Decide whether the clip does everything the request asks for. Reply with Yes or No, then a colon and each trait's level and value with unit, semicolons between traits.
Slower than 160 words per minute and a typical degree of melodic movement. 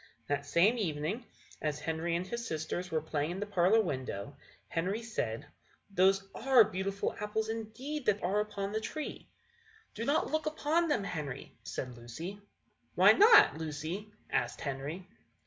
No: average, 150 wpm; wide, 5.9 semitones